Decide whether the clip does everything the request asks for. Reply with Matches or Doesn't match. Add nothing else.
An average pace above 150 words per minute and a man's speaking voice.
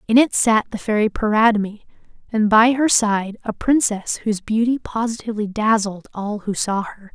Doesn't match